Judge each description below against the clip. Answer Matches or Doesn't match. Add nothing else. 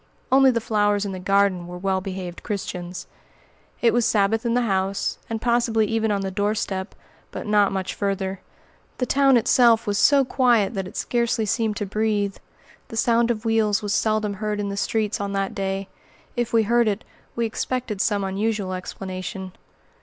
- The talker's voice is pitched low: Doesn't match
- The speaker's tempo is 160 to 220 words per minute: Matches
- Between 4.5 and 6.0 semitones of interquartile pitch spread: Doesn't match